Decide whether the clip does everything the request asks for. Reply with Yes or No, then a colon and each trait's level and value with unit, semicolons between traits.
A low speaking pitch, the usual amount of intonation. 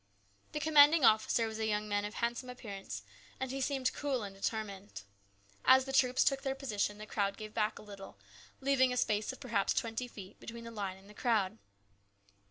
No: high, 225 Hz; average, 4.0 semitones